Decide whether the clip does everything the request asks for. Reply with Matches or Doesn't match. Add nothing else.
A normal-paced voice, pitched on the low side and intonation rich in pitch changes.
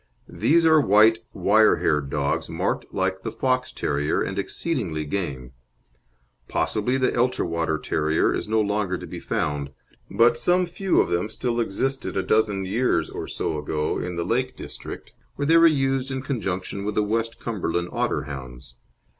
Matches